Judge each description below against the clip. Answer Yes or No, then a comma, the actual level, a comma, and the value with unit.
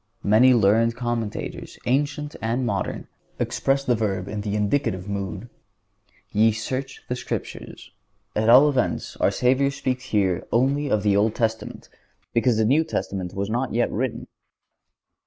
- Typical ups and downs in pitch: Yes, average, 3.8 semitones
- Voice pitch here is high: No, low, 115 Hz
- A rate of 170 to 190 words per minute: No, average, 145 wpm